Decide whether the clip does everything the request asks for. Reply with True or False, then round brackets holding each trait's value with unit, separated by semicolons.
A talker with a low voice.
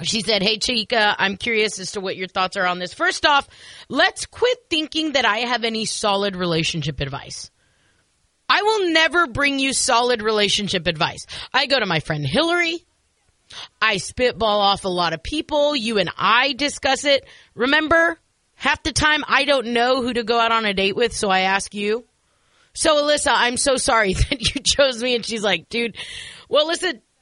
False (235 Hz)